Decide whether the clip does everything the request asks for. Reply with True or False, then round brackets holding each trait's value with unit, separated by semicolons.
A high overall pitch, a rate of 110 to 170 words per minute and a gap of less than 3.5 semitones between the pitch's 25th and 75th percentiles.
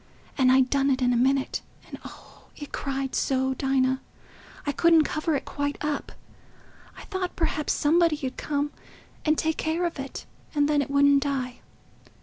True (285 Hz; 160 wpm; 2.4 semitones)